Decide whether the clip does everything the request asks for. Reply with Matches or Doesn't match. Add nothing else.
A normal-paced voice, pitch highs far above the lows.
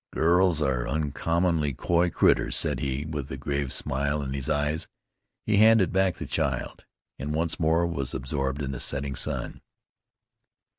Doesn't match